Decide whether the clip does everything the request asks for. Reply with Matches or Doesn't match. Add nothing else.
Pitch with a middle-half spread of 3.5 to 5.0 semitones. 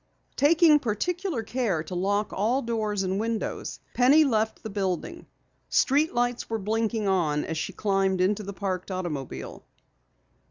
Matches